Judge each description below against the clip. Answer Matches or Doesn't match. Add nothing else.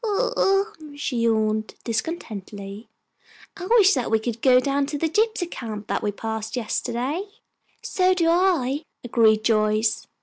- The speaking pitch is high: Matches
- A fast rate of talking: Doesn't match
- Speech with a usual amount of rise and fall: Doesn't match